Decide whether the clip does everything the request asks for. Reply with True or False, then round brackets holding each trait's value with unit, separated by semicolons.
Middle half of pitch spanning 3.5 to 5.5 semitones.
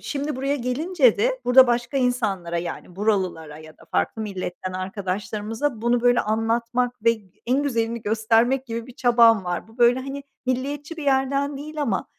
True (4.0 semitones)